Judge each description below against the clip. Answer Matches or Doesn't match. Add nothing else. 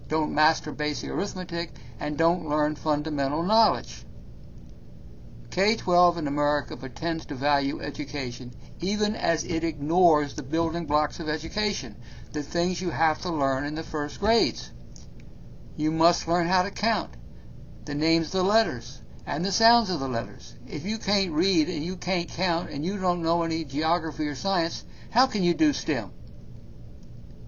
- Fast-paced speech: Doesn't match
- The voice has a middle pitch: Matches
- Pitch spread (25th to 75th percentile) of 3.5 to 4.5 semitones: Matches